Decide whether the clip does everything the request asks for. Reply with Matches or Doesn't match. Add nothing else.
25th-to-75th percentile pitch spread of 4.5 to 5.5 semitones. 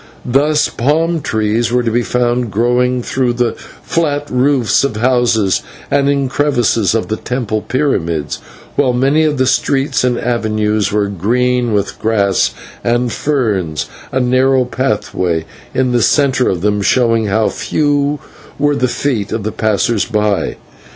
Doesn't match